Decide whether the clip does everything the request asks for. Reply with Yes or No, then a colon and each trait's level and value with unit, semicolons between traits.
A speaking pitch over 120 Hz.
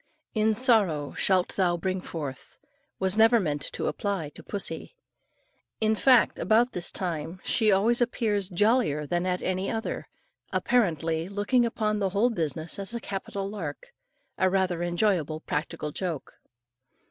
Yes: high, 190 Hz